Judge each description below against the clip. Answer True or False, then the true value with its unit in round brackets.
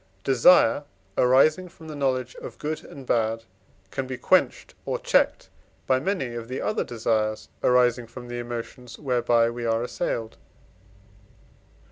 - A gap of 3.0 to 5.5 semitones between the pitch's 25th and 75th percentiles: False (2.5 semitones)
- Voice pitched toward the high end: False (125 Hz)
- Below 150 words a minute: True (140 wpm)